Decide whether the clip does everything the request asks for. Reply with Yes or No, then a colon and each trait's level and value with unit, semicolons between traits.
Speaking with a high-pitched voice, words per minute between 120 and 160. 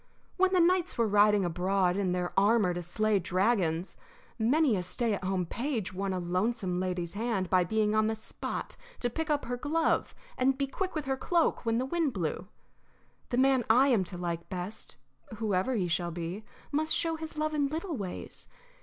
No: high, 215 Hz; average, 195 wpm